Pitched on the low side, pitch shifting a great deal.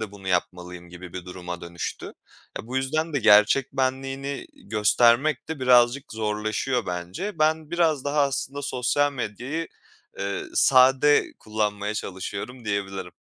Yes: low, 120 Hz; wide, 5.8 semitones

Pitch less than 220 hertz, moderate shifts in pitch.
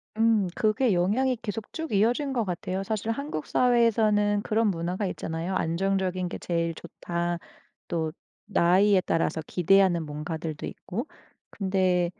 Yes: high, 190 Hz; average, 4.1 semitones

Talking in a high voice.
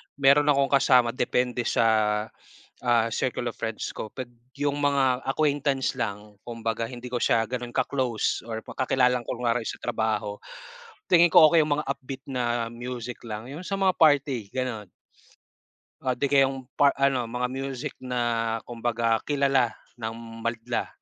No: low, 125 Hz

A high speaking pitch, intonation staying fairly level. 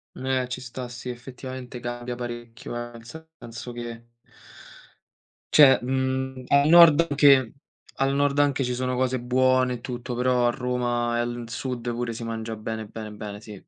No: low, 125 Hz; narrow, 1.7 semitones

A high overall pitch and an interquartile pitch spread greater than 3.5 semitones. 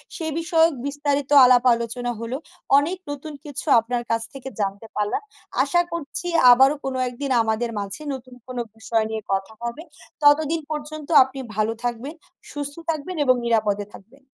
Yes: very high, 260 Hz; average, 4.2 semitones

